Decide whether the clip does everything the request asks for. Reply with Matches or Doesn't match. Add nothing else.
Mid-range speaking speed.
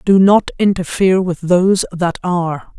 Matches